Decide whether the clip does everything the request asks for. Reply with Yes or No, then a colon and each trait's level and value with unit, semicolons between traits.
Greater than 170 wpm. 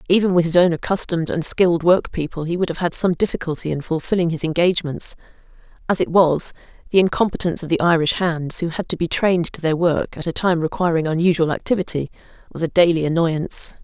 Yes: average, 195 wpm